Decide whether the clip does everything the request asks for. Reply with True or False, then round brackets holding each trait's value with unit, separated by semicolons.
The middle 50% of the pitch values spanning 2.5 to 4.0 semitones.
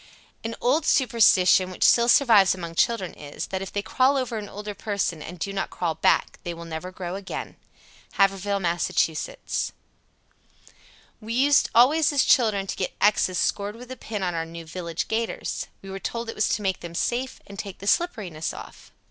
False (4.4 semitones)